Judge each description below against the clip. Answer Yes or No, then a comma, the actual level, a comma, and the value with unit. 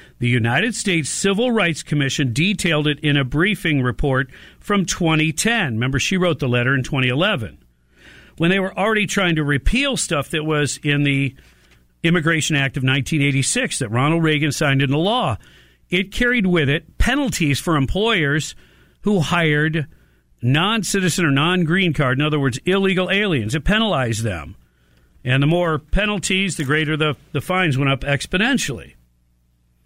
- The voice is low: No, medium, 150 Hz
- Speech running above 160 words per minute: No, average, 155 wpm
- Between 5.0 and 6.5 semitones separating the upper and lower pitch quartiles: Yes, wide, 5.6 semitones